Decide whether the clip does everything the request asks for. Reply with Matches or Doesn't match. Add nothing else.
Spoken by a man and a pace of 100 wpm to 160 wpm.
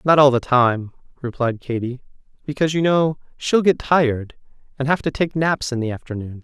Doesn't match